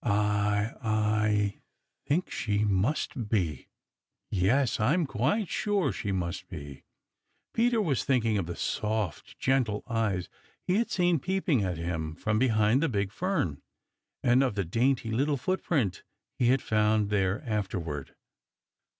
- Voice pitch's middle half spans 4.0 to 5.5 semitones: Yes, average, 5.2 semitones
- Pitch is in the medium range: No, low, 110 Hz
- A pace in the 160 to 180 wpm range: No, average, 140 wpm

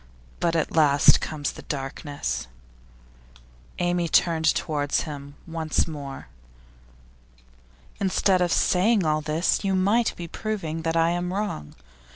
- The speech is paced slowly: Yes, slow, 125 wpm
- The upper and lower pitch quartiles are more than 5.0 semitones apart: No, average, 3.3 semitones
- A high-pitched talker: No, medium, 165 Hz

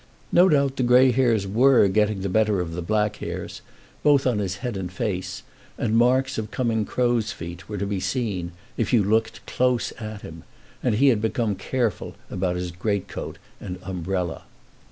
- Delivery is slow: No, average, 185 wpm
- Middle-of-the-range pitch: No, low, 105 Hz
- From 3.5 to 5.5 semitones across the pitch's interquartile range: Yes, average, 4.4 semitones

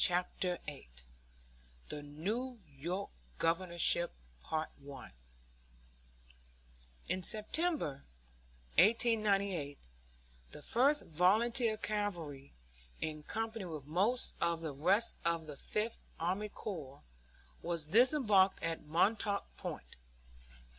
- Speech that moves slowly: Yes, slow, 85 wpm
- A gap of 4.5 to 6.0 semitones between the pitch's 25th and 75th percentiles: Yes, average, 5.3 semitones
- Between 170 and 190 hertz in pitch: Yes, medium, 185 Hz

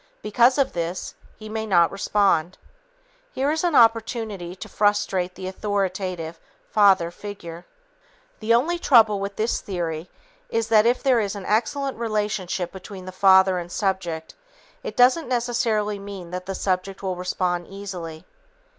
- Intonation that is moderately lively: Yes, average, 3.5 semitones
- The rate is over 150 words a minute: No, average, 145 wpm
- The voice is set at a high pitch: Yes, high, 200 Hz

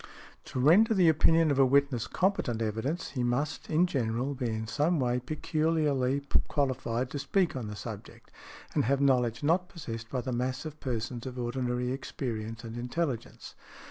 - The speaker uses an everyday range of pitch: Yes, average, 4.1 semitones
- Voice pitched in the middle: No, low, 130 Hz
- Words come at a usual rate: Yes, average, 170 wpm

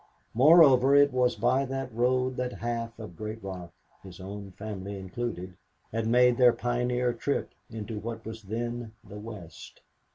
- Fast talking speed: No, average, 155 wpm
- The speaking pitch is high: No, low, 115 Hz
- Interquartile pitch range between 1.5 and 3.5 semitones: Yes, average, 3.2 semitones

